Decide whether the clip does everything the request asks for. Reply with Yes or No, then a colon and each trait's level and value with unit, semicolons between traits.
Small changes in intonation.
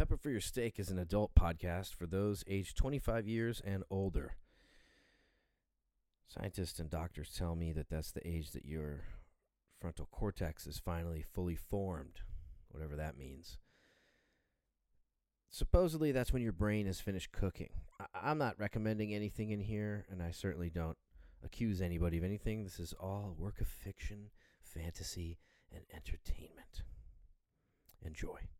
No: average, 4.1 semitones